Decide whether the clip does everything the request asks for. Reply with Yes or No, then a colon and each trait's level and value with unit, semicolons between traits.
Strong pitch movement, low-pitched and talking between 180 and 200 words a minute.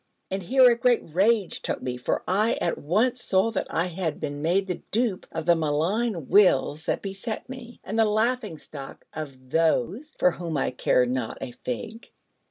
No: wide, 6.5 semitones; medium, 185 Hz; average, 185 wpm